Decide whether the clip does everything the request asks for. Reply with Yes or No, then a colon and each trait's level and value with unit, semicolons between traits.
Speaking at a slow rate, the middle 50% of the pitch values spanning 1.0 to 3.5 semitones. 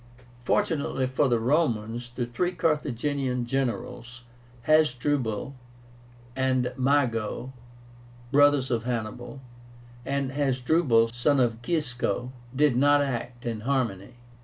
Yes: slow, 100 wpm; average, 3.1 semitones